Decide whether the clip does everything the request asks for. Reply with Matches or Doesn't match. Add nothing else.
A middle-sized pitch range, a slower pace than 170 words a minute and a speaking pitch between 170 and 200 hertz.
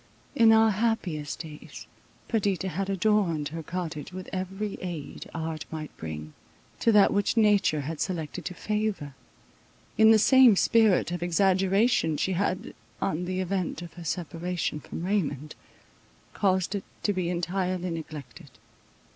Matches